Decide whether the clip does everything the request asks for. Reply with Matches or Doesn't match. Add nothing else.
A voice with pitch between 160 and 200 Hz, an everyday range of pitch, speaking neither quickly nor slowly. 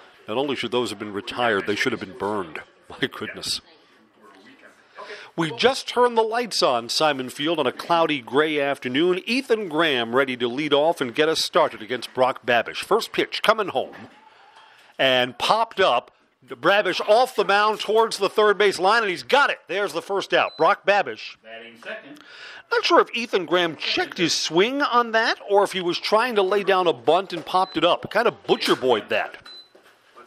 Doesn't match